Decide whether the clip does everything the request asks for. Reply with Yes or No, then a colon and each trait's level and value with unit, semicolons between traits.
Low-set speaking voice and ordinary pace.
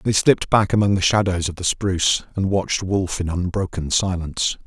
Yes: very low, 95 Hz; average, 195 wpm